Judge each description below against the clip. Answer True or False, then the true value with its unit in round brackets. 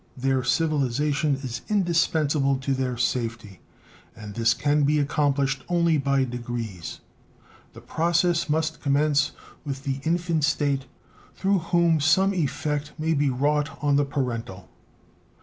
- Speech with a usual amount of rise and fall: True (3.3 semitones)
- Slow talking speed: True (130 wpm)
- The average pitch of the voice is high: False (145 Hz)